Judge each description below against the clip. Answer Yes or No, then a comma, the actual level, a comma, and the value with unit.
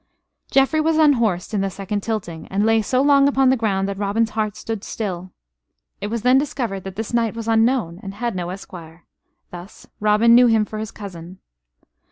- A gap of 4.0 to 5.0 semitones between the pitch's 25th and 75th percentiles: No, average, 3.4 semitones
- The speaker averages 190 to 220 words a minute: Yes, average, 195 wpm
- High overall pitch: Yes, high, 215 Hz